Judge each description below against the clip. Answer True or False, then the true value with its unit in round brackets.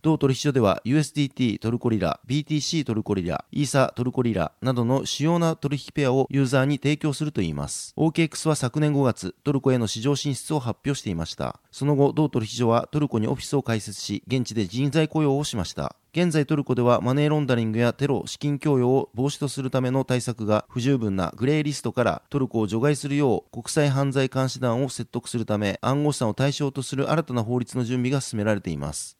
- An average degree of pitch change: True (4.0 semitones)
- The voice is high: False (130 Hz)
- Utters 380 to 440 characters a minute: True (435 characters per minute)